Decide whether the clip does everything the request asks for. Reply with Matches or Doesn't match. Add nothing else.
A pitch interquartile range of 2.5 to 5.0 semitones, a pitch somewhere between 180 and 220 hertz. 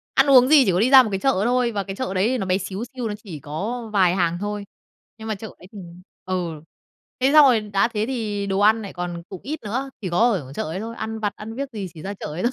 Matches